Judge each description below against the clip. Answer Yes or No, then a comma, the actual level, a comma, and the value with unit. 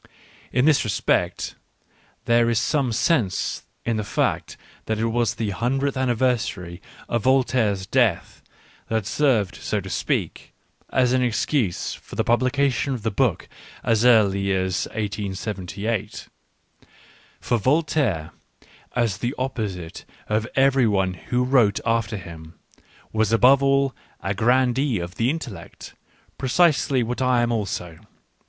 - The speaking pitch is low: Yes, low, 115 Hz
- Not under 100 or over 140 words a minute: Yes, slow, 135 wpm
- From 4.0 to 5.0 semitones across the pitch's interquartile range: Yes, average, 4.4 semitones